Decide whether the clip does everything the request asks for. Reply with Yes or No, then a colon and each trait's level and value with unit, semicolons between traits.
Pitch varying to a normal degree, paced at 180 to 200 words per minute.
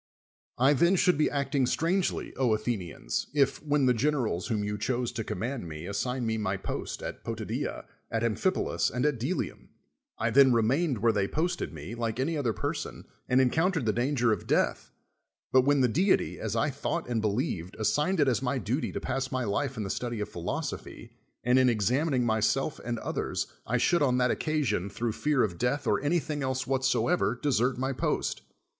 Yes: average, 4.4 semitones; average, 190 wpm